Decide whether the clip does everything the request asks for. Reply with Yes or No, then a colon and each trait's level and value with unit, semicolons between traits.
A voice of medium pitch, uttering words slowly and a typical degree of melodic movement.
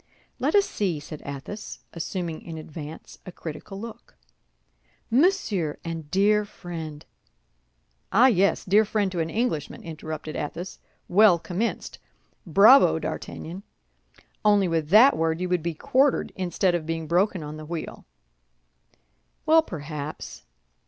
Yes: medium, 175 Hz; slow, 130 wpm; average, 4.6 semitones